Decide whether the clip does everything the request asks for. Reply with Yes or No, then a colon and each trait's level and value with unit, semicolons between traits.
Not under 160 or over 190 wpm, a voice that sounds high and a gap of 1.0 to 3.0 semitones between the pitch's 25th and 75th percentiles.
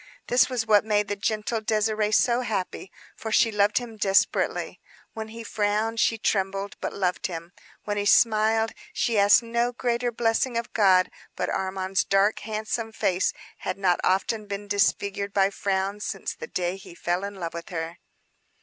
Yes: average, 170 wpm; high, 205 Hz; narrow, 2.4 semitones